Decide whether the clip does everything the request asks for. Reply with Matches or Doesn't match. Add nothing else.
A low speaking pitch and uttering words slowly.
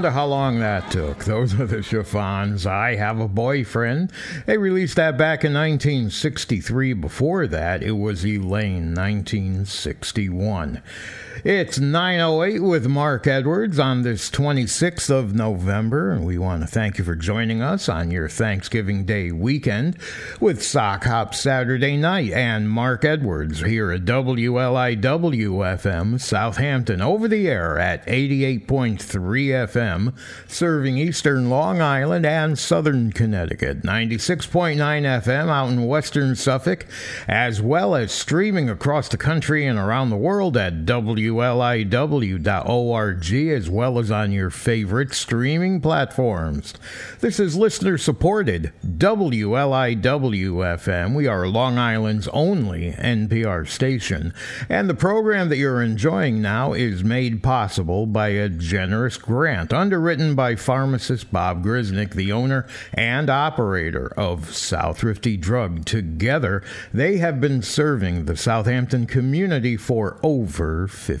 Matches